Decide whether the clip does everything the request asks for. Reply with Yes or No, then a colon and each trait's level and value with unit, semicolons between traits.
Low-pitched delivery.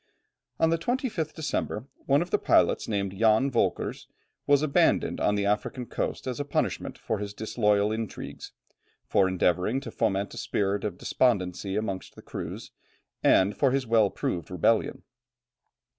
Yes: low, 110 Hz